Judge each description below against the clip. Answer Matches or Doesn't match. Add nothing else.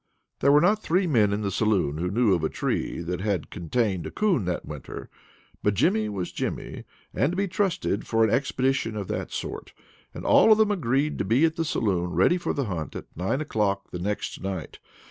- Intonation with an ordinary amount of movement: Doesn't match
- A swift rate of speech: Matches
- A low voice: Matches